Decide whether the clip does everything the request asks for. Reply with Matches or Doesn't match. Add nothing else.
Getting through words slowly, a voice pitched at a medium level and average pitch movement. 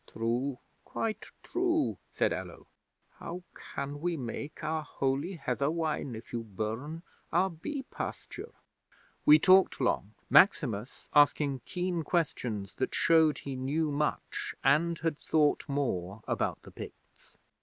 Matches